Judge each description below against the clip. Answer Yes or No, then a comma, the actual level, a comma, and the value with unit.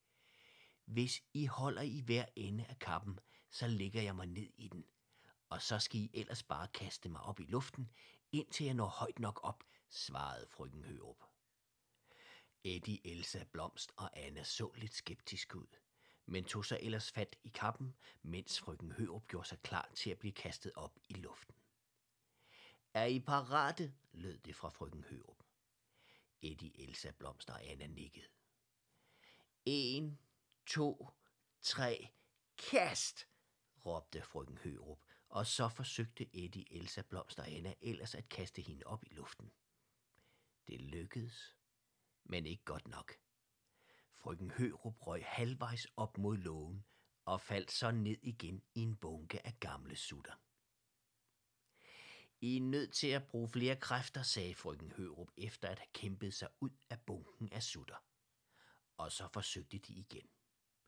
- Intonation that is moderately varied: Yes, average, 4.8 semitones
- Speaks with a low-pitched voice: Yes, low, 110 Hz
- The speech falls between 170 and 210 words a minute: No, average, 150 wpm